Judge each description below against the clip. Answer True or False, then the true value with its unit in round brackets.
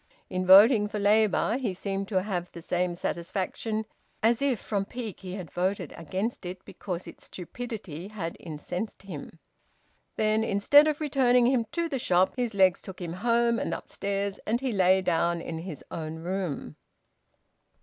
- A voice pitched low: False (195 Hz)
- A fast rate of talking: False (165 wpm)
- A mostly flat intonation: False (4.1 semitones)